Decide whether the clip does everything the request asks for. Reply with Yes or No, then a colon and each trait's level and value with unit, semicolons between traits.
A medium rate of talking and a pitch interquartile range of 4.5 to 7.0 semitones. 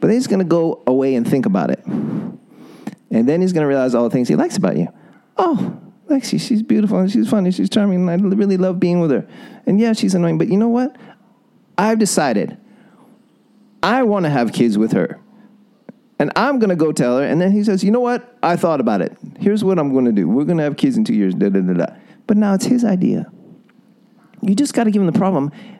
No: fast, 235 wpm; average, 4.8 semitones